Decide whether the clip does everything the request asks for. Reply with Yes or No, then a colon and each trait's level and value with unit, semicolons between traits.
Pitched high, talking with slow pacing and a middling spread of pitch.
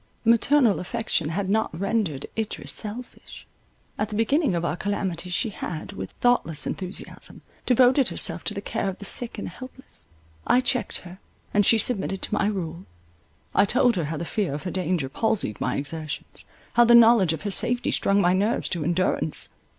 No: high, 200 Hz; average, 180 wpm; average, 4.9 semitones